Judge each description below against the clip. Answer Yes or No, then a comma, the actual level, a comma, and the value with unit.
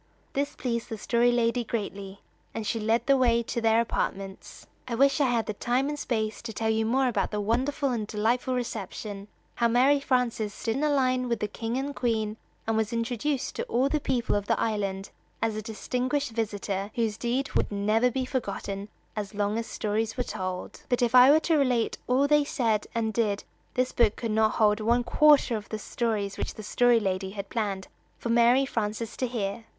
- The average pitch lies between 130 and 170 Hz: No, high, 230 Hz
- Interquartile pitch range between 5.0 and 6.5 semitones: No, average, 3.0 semitones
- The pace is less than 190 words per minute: No, fast, 205 wpm